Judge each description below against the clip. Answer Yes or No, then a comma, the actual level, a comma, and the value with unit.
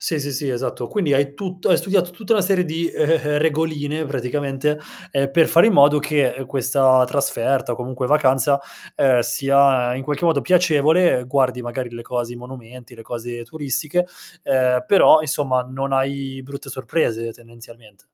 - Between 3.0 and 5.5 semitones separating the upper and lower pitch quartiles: Yes, average, 3.3 semitones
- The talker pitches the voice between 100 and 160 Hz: Yes, low, 135 Hz